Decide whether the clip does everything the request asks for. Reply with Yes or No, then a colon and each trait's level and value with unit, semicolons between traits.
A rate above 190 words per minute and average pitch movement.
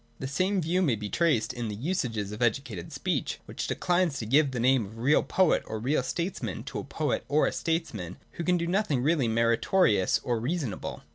No: fast, 205 wpm; wide, 7.0 semitones